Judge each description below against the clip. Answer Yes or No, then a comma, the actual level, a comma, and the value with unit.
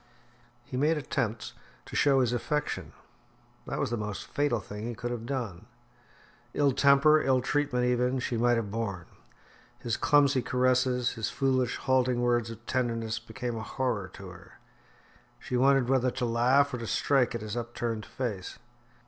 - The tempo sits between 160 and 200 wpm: Yes, average, 165 wpm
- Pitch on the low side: Yes, low, 125 Hz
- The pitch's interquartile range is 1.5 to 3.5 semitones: Yes, narrow, 2.6 semitones